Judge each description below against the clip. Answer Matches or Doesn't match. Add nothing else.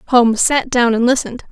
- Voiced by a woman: Matches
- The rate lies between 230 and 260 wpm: Doesn't match